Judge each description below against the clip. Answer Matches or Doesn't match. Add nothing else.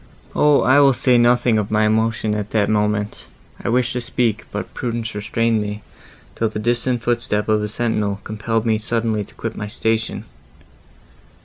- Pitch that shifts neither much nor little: Doesn't match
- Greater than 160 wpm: Matches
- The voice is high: Doesn't match